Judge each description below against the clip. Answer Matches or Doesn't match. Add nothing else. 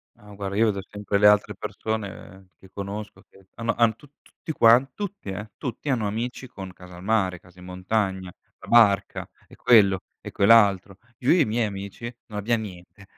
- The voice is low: Matches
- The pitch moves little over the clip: Doesn't match